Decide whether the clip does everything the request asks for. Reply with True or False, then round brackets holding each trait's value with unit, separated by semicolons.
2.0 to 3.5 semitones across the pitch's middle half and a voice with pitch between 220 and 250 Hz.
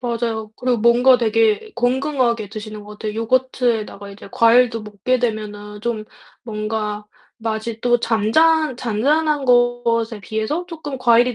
True (2.6 semitones; 230 Hz)